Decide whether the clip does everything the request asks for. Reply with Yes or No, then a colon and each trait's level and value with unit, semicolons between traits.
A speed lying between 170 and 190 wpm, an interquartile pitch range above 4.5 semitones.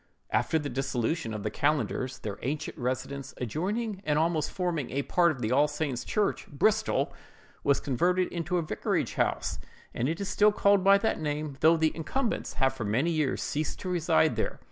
Yes: average, 185 wpm; average, 5.0 semitones